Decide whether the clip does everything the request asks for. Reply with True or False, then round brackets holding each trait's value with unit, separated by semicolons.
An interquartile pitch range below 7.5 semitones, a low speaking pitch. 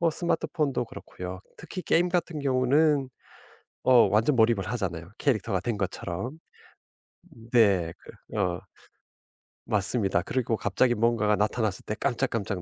True (5.1 semitones; 115 Hz)